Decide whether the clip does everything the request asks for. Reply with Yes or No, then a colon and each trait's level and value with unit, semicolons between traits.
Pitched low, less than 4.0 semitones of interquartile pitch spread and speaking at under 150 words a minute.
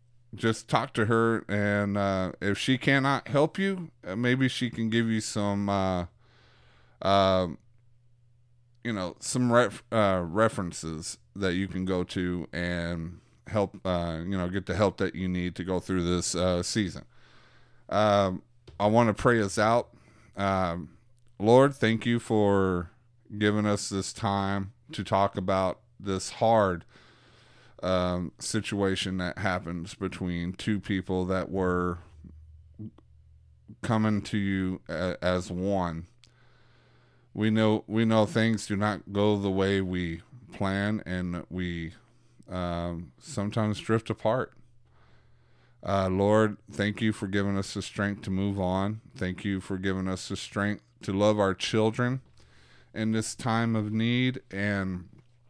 Yes: low, 100 Hz; average, 3.6 semitones; average, 140 wpm